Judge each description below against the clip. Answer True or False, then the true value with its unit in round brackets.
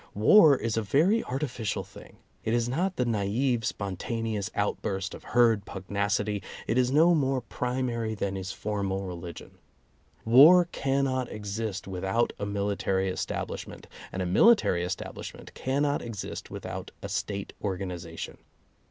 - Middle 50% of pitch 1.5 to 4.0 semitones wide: False (4.8 semitones)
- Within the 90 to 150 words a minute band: True (140 wpm)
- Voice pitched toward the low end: True (110 Hz)